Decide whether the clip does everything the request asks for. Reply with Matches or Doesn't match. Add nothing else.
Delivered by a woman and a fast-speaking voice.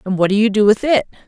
Matches